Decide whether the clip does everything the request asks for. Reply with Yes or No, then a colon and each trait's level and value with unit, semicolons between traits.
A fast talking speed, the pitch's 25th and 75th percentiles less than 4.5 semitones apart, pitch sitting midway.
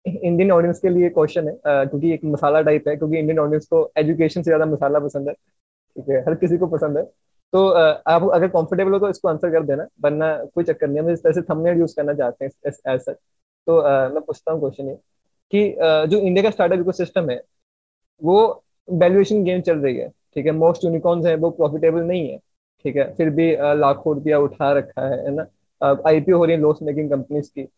Yes: fast, 210 wpm; average, 2.9 semitones; medium, 160 Hz